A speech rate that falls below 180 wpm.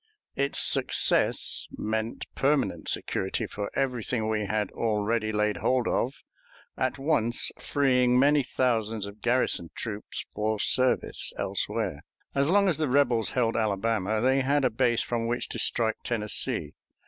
Yes: average, 140 wpm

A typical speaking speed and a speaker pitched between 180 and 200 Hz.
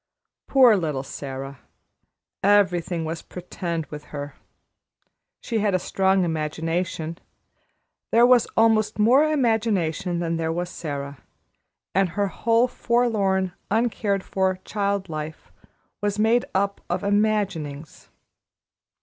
No: slow, 110 wpm; high, 190 Hz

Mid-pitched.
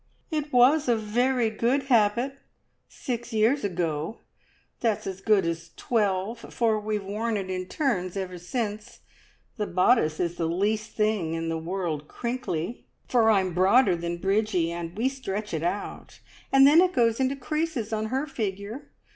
No: high, 215 Hz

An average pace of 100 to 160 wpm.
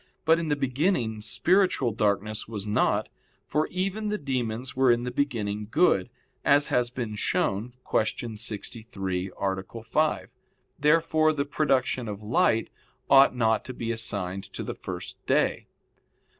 Yes: average, 145 wpm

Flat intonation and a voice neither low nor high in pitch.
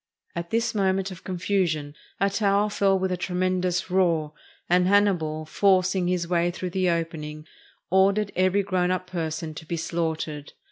Yes: narrow, 2.3 semitones; medium, 180 Hz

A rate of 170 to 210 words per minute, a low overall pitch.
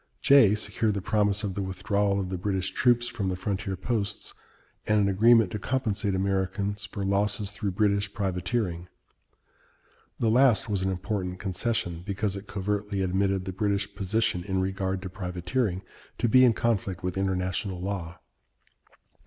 No: average, 155 wpm; low, 100 Hz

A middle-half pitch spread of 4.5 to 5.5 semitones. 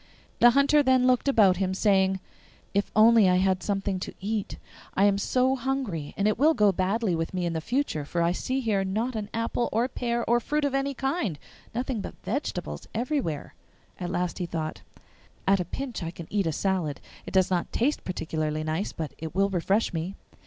Yes: average, 5.2 semitones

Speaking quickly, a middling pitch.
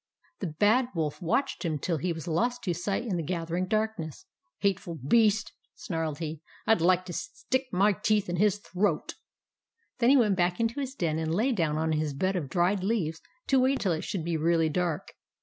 Yes: fast, 220 wpm; medium, 180 Hz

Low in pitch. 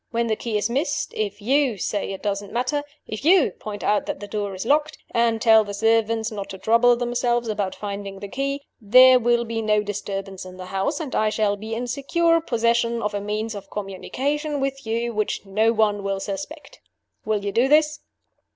No: high, 225 Hz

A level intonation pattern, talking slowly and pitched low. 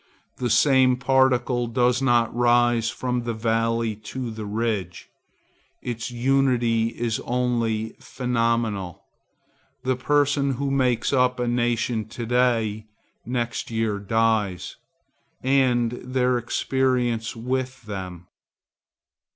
Yes: narrow, 2.0 semitones; slow, 105 wpm; low, 120 Hz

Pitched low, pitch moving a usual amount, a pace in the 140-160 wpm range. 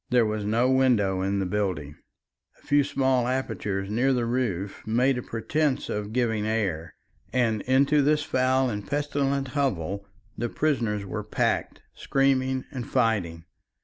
Yes: low, 120 Hz; average, 4.4 semitones; average, 145 wpm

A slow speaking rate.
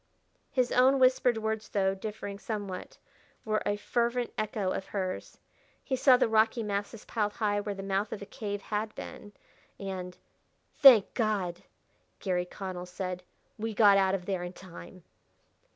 No: average, 155 wpm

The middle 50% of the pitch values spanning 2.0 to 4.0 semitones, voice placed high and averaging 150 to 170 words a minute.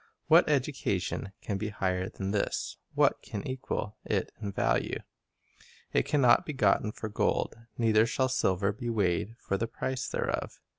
No: average, 3.1 semitones; low, 105 Hz; average, 160 wpm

